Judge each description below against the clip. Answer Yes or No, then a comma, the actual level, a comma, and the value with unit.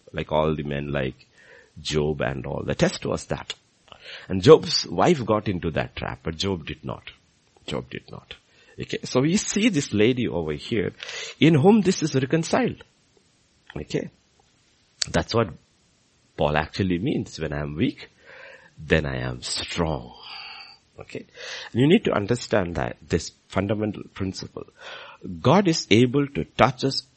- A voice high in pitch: No, very low, 95 Hz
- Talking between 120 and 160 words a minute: Yes, average, 150 wpm